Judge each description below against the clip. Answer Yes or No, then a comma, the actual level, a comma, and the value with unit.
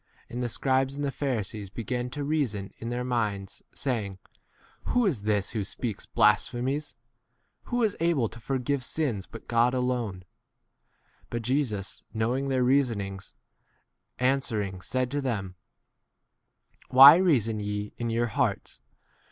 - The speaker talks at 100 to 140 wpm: No, average, 160 wpm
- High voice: No, low, 120 Hz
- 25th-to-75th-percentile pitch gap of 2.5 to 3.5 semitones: No, average, 4.3 semitones